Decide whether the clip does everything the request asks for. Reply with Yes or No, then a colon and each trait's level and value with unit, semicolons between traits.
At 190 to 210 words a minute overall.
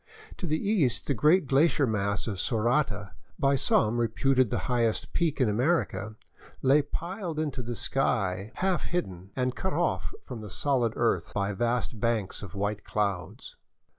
No: average, 160 wpm